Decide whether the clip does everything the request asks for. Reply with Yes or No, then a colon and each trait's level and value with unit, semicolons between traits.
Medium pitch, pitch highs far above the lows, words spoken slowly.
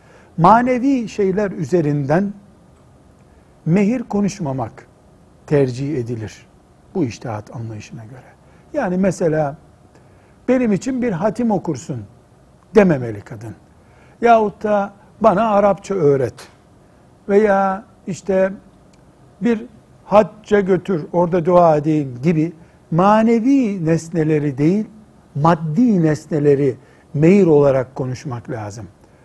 Yes: medium, 170 Hz; wide, 6.4 semitones; slow, 90 wpm